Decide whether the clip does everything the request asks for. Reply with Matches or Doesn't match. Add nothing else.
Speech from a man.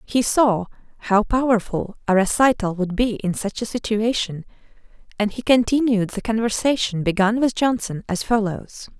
Doesn't match